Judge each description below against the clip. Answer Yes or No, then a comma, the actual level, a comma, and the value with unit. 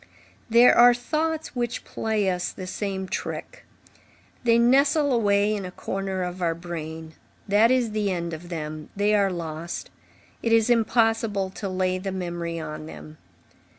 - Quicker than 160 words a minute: No, average, 155 wpm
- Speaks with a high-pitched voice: Yes, high, 195 Hz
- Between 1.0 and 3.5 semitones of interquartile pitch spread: No, average, 4.8 semitones